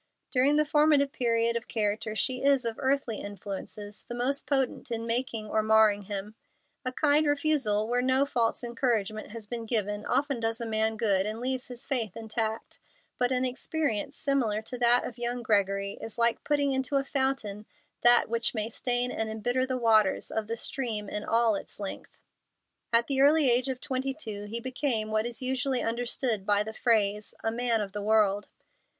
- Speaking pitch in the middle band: No, high, 235 Hz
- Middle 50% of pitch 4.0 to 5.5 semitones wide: No, average, 3.2 semitones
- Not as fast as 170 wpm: No, average, 185 wpm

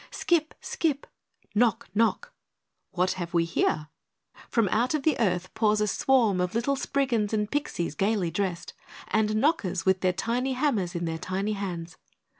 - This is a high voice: Yes, high, 210 Hz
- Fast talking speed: No, average, 160 wpm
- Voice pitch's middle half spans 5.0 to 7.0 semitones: Yes, wide, 5.4 semitones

